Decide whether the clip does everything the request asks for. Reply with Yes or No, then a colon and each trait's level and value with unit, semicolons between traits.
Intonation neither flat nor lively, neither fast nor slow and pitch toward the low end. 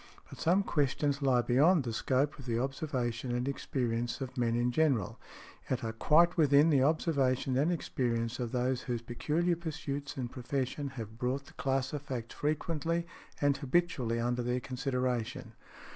Yes: average, 3.2 semitones; average, 160 wpm; low, 130 Hz